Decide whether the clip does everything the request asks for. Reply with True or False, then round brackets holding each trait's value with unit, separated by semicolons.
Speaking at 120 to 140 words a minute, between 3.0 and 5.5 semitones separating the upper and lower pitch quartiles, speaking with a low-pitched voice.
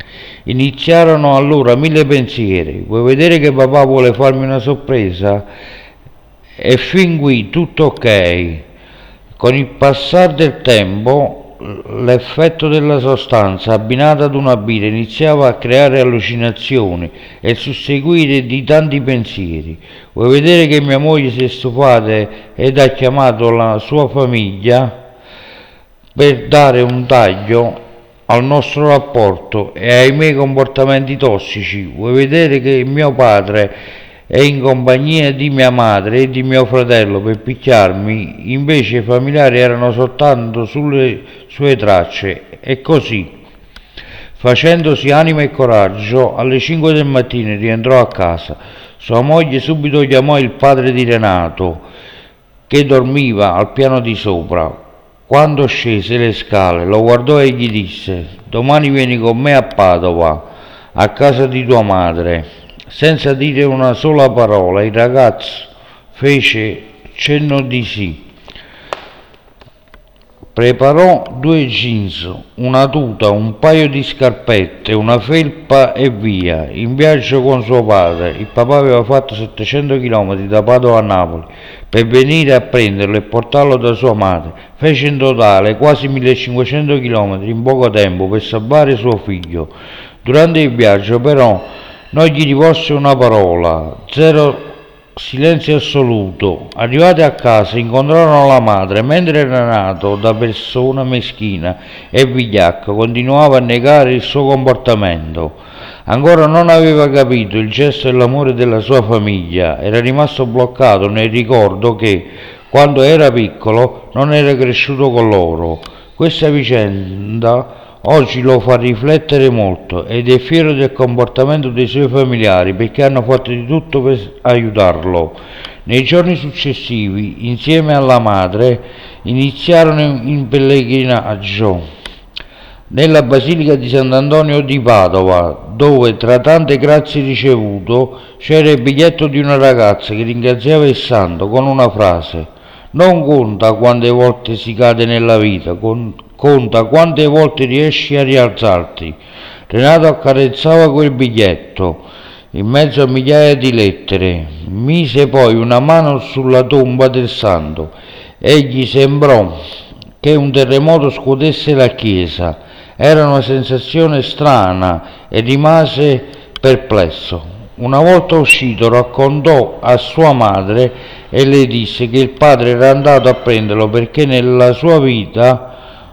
True (130 wpm; 4.4 semitones; 125 Hz)